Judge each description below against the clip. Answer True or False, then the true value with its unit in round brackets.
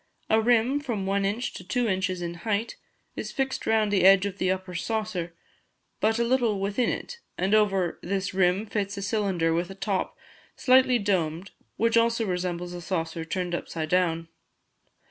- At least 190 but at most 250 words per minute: False (175 wpm)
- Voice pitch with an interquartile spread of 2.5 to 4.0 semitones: True (3.7 semitones)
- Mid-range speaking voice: False (195 Hz)